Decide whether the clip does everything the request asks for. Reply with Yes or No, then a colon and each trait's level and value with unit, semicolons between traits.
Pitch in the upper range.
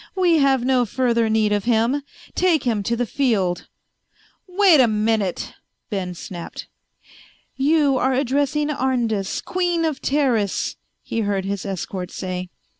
Yes: high, 240 Hz